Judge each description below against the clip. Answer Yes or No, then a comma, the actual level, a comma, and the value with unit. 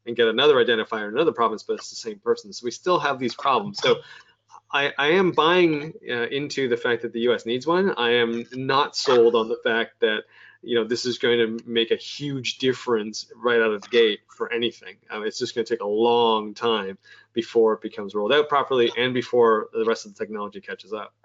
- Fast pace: Yes, fast, 230 wpm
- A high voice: No, low, 125 Hz